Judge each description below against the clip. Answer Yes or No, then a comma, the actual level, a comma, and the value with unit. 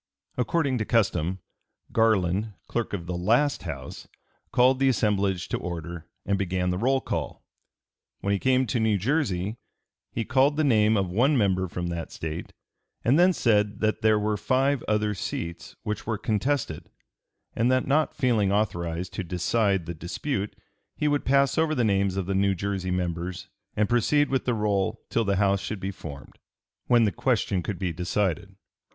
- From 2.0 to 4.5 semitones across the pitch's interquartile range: No, average, 5.0 semitones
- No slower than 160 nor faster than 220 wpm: Yes, average, 175 wpm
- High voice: No, low, 105 Hz